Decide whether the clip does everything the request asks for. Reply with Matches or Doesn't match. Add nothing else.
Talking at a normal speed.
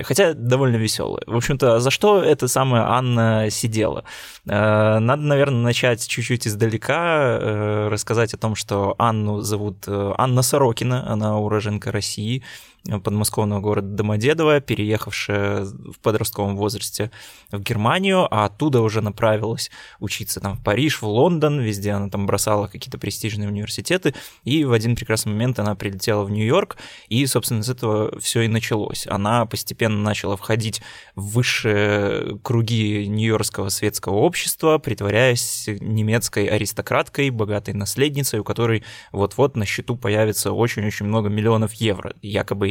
Matches